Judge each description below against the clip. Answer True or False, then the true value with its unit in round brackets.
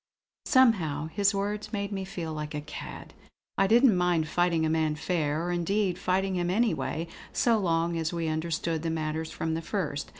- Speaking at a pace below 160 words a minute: False (180 wpm)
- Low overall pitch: False (170 Hz)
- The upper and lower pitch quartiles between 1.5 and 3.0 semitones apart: False (3.6 semitones)